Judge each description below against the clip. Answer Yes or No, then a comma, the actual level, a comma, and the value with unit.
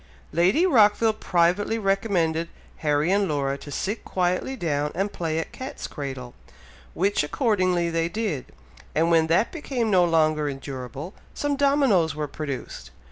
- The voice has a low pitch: No, medium, 170 Hz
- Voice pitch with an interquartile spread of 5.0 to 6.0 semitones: Yes, average, 5.3 semitones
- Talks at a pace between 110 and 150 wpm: Yes, average, 140 wpm